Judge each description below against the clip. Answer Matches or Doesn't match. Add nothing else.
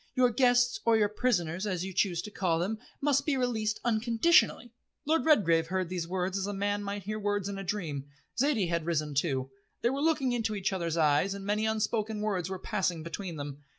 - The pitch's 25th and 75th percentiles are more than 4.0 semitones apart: Matches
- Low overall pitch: Doesn't match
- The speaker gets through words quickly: Matches